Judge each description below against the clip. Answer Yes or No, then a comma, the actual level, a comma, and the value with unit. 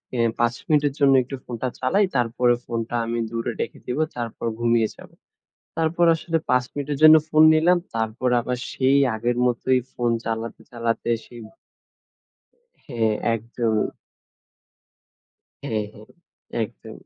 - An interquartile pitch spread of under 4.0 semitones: Yes, average, 3.3 semitones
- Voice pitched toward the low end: Yes, low, 120 Hz